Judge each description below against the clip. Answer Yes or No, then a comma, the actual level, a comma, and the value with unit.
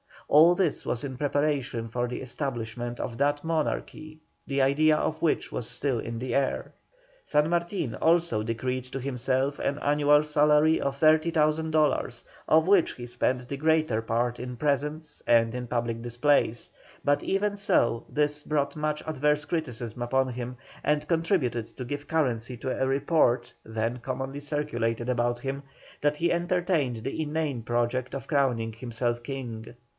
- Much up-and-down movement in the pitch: No, average, 4.0 semitones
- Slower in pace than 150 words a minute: No, average, 155 wpm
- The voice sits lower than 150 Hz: Yes, low, 135 Hz